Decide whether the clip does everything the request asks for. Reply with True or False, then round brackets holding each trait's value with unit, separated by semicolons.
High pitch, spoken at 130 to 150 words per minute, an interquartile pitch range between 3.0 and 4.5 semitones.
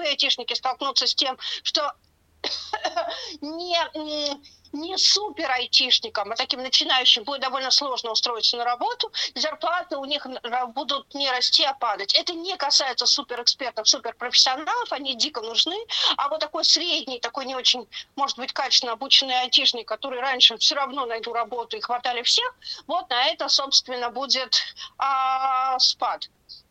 True (270 Hz; 140 wpm; 3.8 semitones)